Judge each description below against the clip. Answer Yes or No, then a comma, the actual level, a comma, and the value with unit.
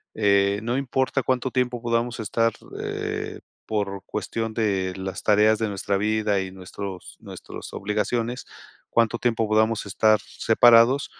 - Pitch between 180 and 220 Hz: No, low, 110 Hz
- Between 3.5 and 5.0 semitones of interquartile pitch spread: No, average, 3.0 semitones